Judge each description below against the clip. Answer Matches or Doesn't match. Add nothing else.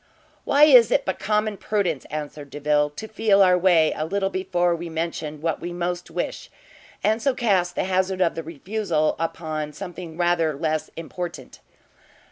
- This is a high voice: Doesn't match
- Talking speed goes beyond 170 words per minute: Doesn't match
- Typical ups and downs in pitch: Matches